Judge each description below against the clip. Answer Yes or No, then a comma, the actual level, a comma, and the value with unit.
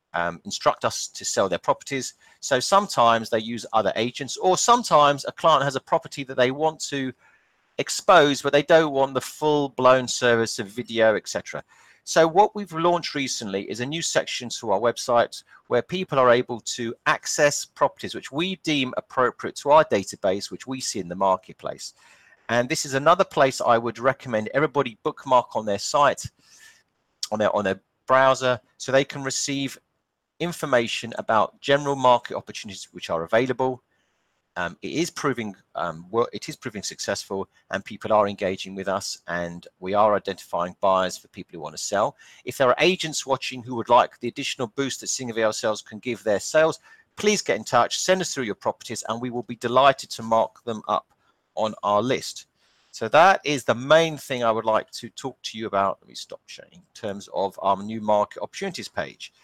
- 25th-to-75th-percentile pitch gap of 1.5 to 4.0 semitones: No, average, 4.6 semitones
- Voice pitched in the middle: No, low, 130 Hz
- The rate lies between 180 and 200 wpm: Yes, average, 190 wpm